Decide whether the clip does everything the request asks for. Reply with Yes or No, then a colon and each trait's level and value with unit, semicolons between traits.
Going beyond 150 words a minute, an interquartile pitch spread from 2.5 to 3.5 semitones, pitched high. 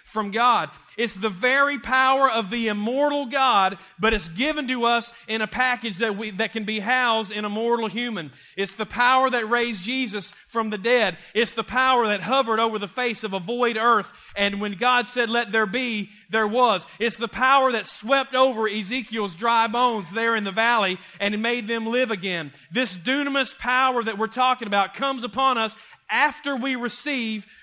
Yes: average, 195 wpm; average, 2.8 semitones; high, 230 Hz